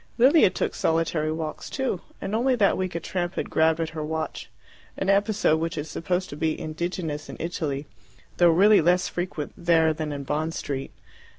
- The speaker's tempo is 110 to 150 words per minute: No, average, 185 wpm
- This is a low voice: No, medium, 165 Hz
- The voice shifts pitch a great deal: No, average, 3.0 semitones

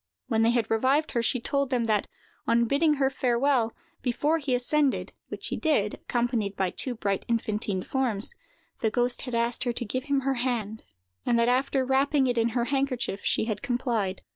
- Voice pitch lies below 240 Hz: No, high, 245 Hz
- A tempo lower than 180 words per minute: No, average, 185 wpm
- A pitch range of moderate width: Yes, average, 3.0 semitones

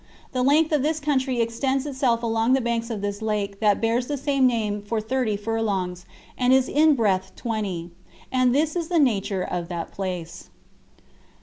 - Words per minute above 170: Yes, average, 180 wpm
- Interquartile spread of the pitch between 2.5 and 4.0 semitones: No, average, 4.6 semitones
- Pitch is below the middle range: No, high, 230 Hz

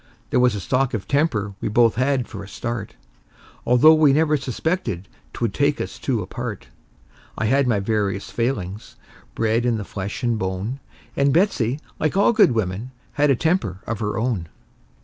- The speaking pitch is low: Yes, low, 120 Hz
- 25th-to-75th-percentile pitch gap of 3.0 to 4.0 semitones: No, average, 5.1 semitones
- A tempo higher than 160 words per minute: Yes, average, 175 wpm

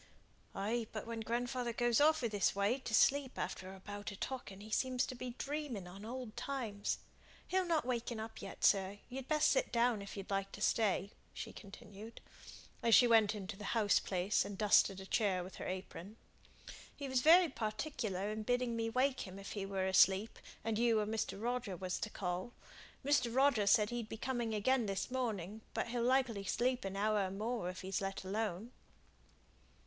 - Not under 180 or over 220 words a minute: Yes, average, 195 wpm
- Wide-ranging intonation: No, average, 3.8 semitones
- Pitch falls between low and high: No, high, 220 Hz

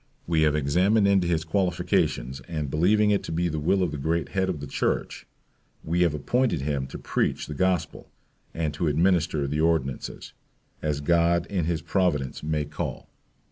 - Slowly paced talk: No, average, 180 wpm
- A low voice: Yes, very low, 80 Hz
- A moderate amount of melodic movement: Yes, average, 3.3 semitones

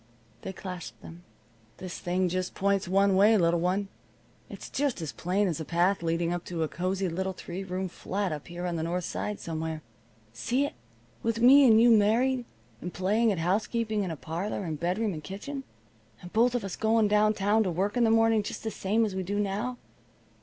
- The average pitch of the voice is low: No, high, 195 Hz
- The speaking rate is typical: No, fast, 210 wpm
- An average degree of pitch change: Yes, average, 3.8 semitones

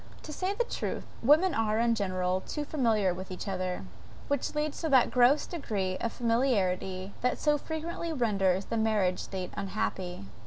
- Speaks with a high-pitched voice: Yes, high, 220 Hz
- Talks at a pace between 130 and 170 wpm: Yes, average, 165 wpm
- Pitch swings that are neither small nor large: No, wide, 7.2 semitones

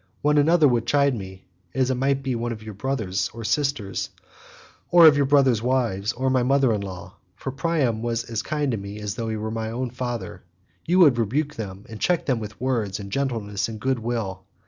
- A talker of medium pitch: No, low, 120 Hz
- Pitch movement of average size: Yes, average, 4.2 semitones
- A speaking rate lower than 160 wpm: No, fast, 205 wpm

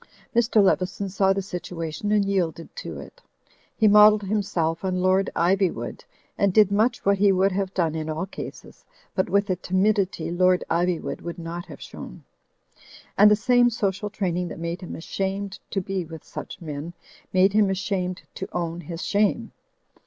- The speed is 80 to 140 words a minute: No, average, 175 wpm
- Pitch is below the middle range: No, high, 190 Hz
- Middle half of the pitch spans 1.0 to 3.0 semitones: Yes, narrow, 2.6 semitones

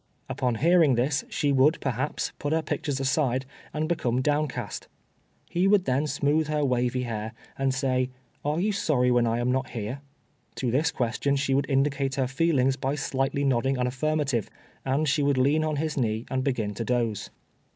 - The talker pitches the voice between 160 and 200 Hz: No, low, 135 Hz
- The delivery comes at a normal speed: Yes, average, 180 wpm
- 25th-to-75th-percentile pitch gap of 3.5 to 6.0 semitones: No, average, 2.9 semitones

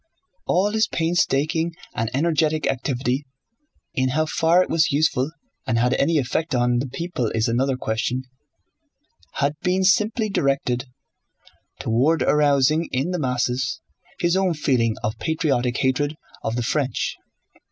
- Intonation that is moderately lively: Yes, average, 4.6 semitones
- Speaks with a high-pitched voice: No, medium, 140 Hz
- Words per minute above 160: No, slow, 135 wpm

